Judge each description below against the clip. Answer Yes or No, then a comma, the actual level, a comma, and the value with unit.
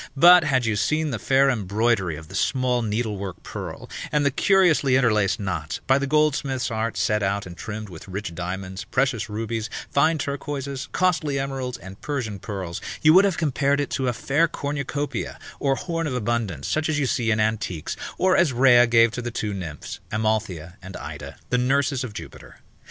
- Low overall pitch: Yes, low, 120 Hz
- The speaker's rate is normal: Yes, average, 185 wpm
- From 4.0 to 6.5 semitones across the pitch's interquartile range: Yes, wide, 5.4 semitones